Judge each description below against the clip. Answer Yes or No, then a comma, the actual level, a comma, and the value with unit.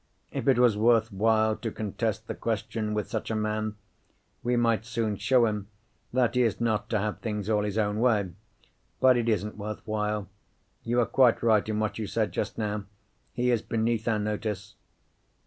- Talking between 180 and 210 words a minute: Yes, average, 190 wpm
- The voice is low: Yes, low, 110 Hz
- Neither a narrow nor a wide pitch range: No, narrow, 1.7 semitones